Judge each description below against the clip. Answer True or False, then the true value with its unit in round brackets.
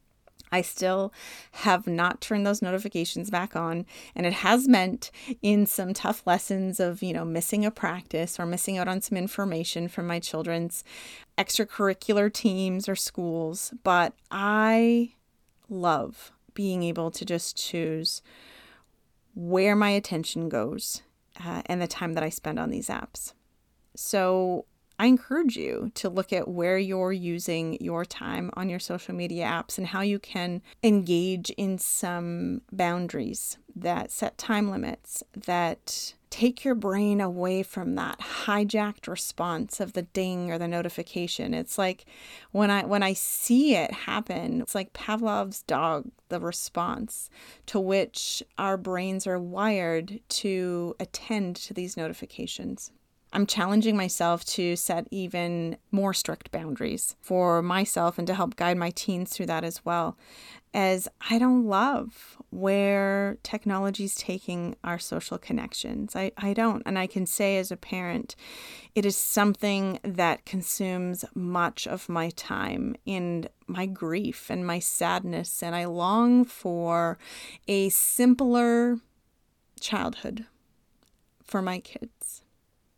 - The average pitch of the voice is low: False (190 Hz)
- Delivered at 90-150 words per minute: True (140 wpm)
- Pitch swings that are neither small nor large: True (3.2 semitones)